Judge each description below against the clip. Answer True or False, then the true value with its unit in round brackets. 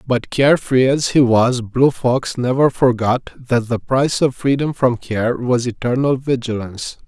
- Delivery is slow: False (170 wpm)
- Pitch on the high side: False (125 Hz)